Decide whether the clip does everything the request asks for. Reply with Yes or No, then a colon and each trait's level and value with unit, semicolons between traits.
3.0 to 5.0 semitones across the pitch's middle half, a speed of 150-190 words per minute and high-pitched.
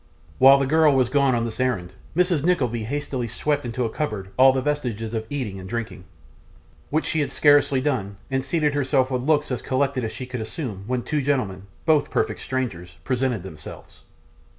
No: average, 4.3 semitones; average, 185 wpm; low, 130 Hz